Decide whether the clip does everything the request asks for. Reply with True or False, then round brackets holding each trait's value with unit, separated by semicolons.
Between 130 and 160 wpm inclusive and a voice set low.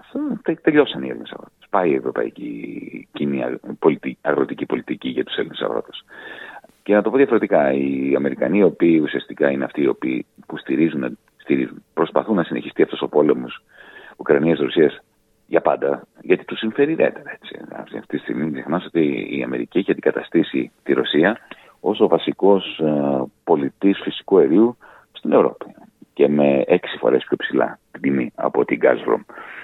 True (150 wpm; 110 Hz)